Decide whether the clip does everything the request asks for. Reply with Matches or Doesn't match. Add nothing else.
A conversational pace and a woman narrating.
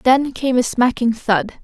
Matches